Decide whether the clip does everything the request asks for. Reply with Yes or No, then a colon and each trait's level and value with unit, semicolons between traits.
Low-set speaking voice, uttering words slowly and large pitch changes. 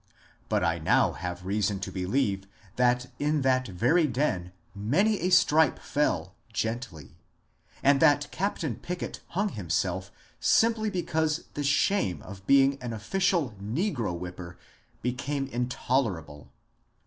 Yes: low, 125 Hz; slow, 125 wpm; wide, 7.9 semitones